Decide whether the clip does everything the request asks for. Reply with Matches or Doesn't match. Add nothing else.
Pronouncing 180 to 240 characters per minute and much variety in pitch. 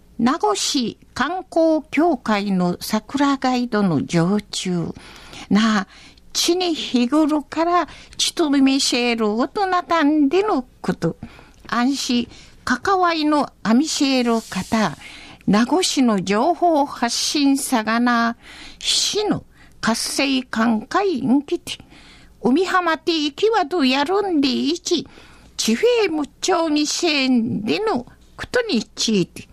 Matches